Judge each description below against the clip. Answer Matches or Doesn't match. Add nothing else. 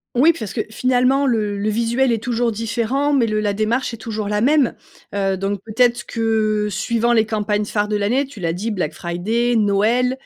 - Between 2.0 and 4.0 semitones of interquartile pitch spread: Matches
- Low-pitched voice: Doesn't match